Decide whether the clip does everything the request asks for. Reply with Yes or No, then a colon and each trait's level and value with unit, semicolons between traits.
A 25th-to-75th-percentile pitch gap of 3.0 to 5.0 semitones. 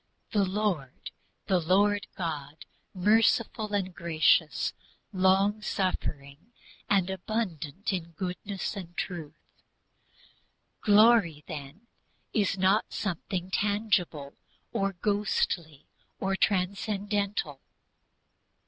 Yes: average, 3.7 semitones